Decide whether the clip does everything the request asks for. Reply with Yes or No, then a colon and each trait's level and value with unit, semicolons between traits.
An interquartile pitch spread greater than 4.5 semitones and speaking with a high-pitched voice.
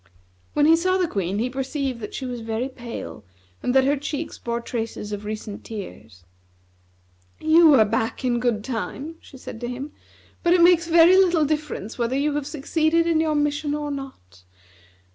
Yes: wide, 5.4 semitones; very high, 270 Hz